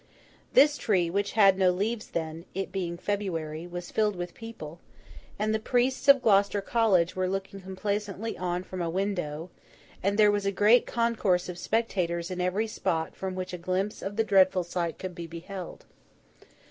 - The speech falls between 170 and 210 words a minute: Yes, average, 175 wpm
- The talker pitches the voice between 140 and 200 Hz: Yes, high, 190 Hz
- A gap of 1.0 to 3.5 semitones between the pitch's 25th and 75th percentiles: Yes, average, 2.8 semitones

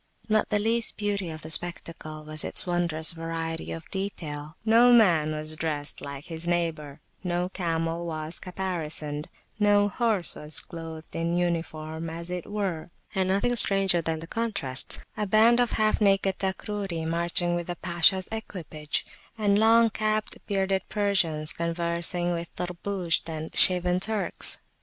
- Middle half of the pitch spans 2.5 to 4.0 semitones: Yes, average, 3.6 semitones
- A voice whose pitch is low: No, medium, 175 Hz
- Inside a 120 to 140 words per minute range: No, average, 150 wpm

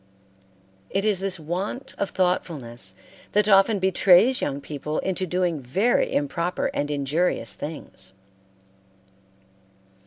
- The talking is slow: Yes, slow, 105 wpm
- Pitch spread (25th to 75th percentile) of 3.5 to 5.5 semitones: Yes, average, 5.2 semitones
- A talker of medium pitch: Yes, medium, 175 Hz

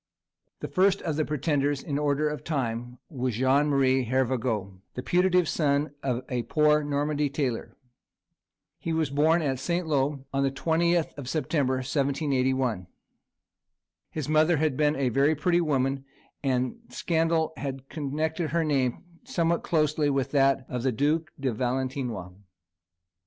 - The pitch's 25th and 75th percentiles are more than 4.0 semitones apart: No, average, 3.0 semitones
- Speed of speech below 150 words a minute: Yes, average, 140 wpm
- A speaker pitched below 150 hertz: Yes, medium, 140 Hz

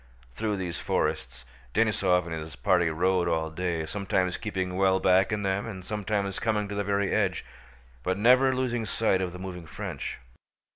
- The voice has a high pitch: No, very low, 95 Hz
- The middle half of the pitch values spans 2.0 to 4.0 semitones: Yes, average, 2.7 semitones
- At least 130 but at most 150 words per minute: No, average, 175 wpm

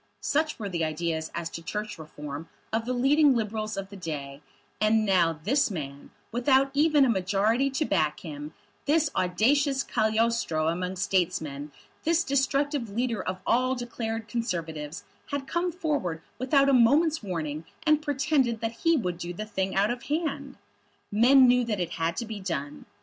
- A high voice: Yes, high, 220 Hz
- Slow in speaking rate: No, average, 165 wpm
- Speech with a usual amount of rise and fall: No, wide, 7.8 semitones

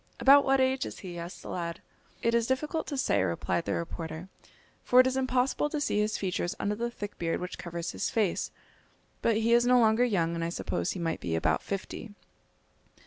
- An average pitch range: No, wide, 6.7 semitones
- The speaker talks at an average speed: No, fast, 210 wpm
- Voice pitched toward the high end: Yes, high, 210 Hz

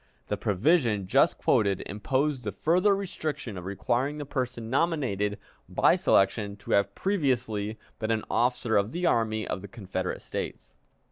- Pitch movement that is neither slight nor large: No, wide, 5.8 semitones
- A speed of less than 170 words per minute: Yes, average, 150 wpm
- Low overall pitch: Yes, low, 115 Hz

